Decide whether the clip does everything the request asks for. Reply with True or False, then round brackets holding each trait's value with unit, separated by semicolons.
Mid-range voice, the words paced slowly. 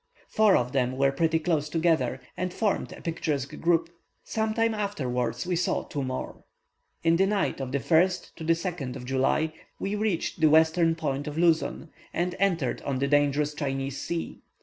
False (160 Hz; 170 wpm)